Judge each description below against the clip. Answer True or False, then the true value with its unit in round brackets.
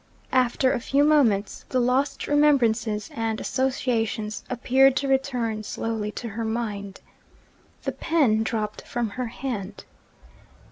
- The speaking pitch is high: True (235 Hz)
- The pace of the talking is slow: True (125 wpm)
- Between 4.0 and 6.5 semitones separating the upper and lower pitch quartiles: False (3.5 semitones)